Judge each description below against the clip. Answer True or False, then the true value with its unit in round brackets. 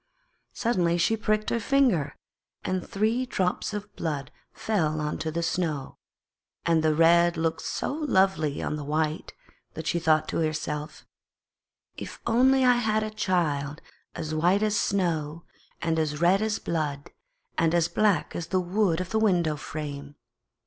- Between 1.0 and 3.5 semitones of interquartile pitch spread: False (5.1 semitones)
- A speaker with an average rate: True (155 wpm)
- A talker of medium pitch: True (170 Hz)